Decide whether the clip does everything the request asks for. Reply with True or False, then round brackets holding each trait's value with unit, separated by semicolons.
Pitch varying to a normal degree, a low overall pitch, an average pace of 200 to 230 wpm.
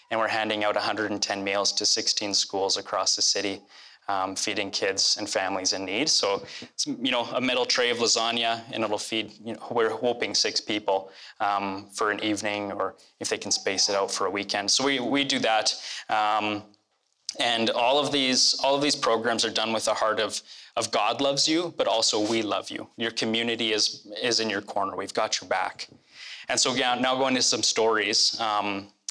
True (3.4 semitones; 110 Hz; 205 wpm)